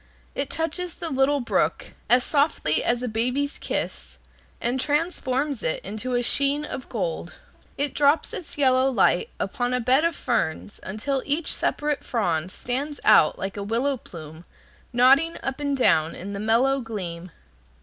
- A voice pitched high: Yes, very high, 255 Hz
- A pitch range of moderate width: Yes, average, 4.3 semitones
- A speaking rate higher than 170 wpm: No, average, 160 wpm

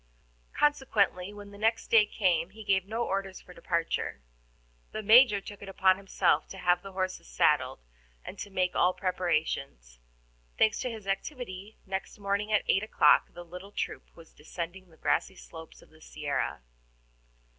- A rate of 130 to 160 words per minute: Yes, average, 155 wpm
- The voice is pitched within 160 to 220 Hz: Yes, high, 190 Hz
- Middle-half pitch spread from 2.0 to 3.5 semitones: Yes, average, 2.9 semitones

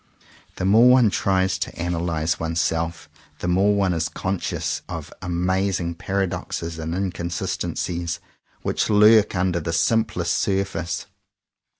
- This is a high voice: No, very low, 90 Hz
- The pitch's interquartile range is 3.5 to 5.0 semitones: No, narrow, 2.5 semitones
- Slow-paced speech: Yes, slow, 115 wpm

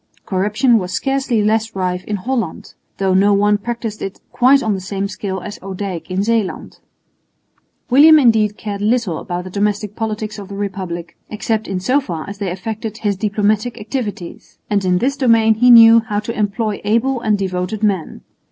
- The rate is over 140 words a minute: Yes, average, 180 wpm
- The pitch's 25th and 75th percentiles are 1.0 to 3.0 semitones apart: Yes, average, 2.7 semitones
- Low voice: No, high, 210 Hz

